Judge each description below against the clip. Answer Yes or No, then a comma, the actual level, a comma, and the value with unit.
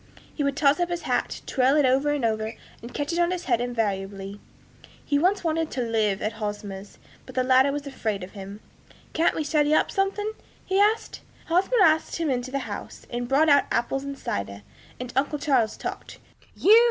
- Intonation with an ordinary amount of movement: No, wide, 6.0 semitones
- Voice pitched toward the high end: Yes, very high, 270 Hz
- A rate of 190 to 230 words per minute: Yes, average, 200 wpm